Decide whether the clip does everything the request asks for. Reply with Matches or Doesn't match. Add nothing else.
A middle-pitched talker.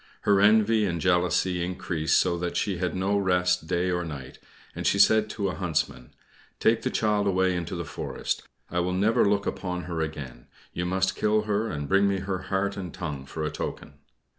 Doesn't match